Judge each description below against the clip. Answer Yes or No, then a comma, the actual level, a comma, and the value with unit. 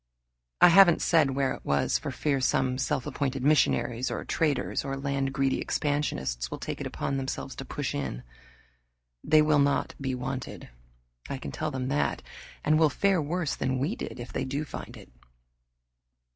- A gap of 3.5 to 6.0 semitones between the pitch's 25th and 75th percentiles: No, narrow, 2.4 semitones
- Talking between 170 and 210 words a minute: Yes, average, 175 wpm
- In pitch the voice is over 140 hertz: No, low, 135 Hz